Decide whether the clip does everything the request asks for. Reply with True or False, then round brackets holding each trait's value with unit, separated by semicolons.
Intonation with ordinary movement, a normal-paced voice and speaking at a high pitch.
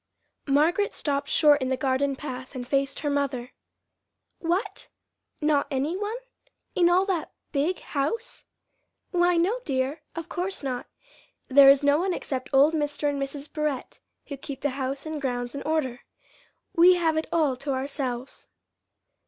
True (3.6 semitones; 155 wpm; 285 Hz)